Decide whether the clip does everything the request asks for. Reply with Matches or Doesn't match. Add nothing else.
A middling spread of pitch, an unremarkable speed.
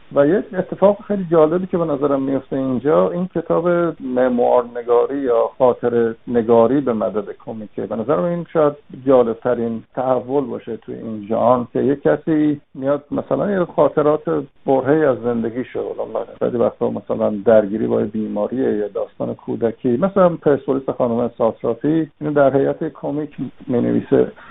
Matches